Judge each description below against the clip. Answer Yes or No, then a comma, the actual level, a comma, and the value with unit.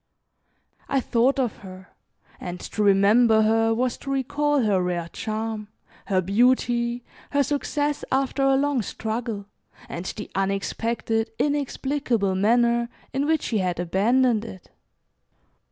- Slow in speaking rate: Yes, slow, 125 wpm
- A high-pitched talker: Yes, high, 230 Hz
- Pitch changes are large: No, average, 4.7 semitones